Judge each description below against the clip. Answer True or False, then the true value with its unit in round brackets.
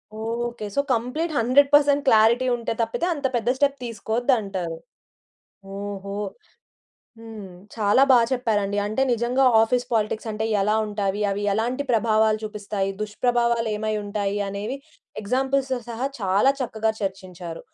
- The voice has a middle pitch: False (225 Hz)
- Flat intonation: False (3.2 semitones)